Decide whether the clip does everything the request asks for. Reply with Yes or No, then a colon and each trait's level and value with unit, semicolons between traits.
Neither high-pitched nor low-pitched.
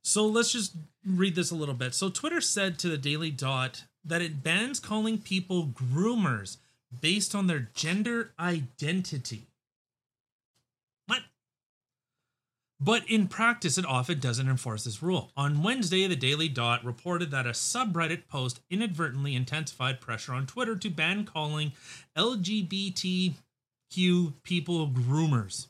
Yes: medium, 160 Hz